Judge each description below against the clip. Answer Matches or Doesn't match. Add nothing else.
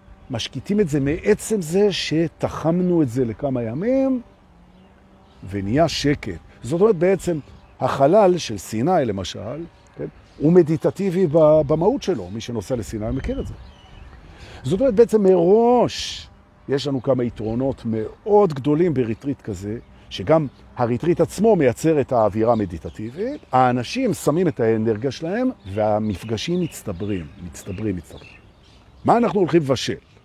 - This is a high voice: Doesn't match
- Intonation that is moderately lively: Doesn't match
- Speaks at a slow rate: Doesn't match